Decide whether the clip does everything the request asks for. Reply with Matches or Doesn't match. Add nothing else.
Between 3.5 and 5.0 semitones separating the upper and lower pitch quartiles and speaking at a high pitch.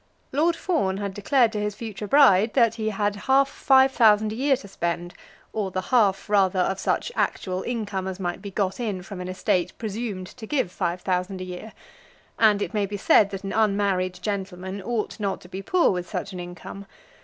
Doesn't match